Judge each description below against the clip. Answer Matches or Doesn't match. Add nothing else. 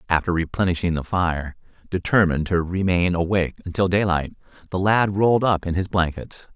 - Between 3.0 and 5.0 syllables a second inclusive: Doesn't match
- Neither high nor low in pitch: Doesn't match